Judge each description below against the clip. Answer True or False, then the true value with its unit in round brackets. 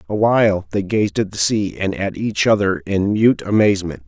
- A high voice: False (100 Hz)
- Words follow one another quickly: False (190 wpm)